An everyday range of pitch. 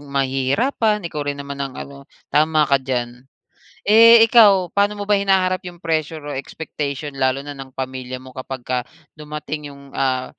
Yes: average, 5.0 semitones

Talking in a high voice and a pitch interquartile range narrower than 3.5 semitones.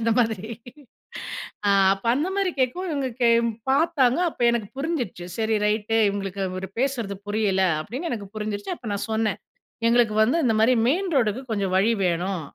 No: high, 220 Hz; average, 4.7 semitones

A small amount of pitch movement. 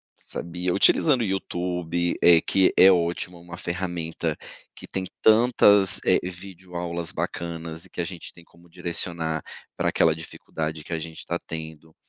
Yes: narrow, 2.0 semitones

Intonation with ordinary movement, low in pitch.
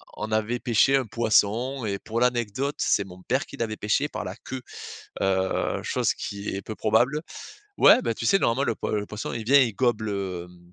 Yes: average, 3.7 semitones; low, 110 Hz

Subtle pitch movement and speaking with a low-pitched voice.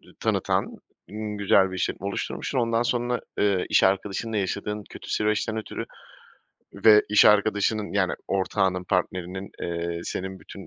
Yes: narrow, 2.2 semitones; low, 100 Hz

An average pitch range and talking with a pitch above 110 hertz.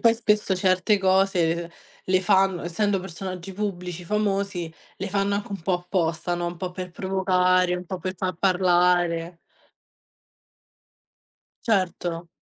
No: narrow, 1.7 semitones; medium, 185 Hz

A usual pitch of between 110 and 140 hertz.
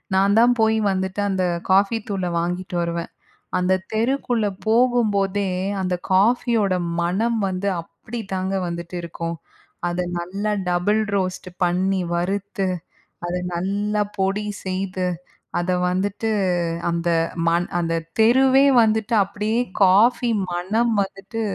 No: high, 195 Hz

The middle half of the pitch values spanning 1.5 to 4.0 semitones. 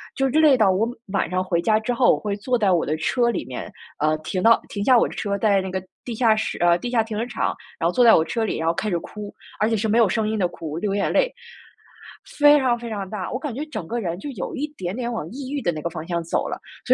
No: average, 4.8 semitones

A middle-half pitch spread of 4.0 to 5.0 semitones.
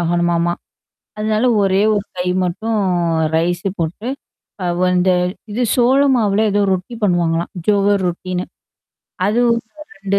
No: average, 3.4 semitones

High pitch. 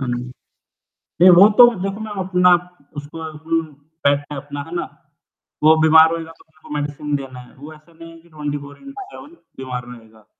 No: medium, 155 Hz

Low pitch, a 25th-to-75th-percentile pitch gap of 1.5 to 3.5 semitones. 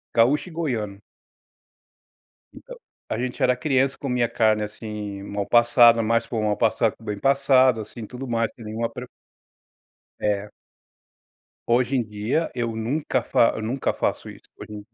Yes: low, 115 Hz; average, 3.0 semitones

